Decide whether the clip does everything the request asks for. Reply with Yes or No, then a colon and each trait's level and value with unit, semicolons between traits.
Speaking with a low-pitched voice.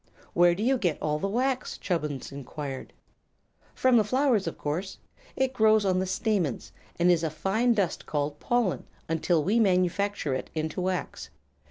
No: medium, 185 Hz